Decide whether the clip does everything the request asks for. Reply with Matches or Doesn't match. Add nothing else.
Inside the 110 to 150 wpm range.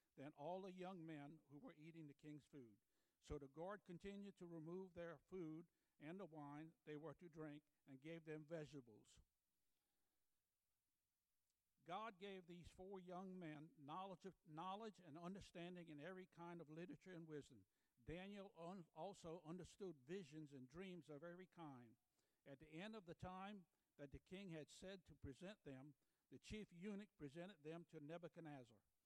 Doesn't match